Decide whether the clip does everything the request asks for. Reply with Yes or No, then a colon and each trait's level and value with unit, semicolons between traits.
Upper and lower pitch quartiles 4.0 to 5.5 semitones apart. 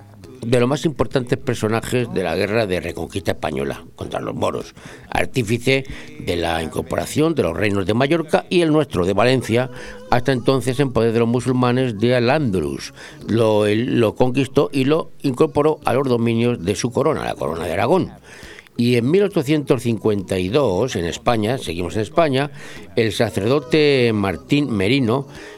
Yes: average, 4.9 semitones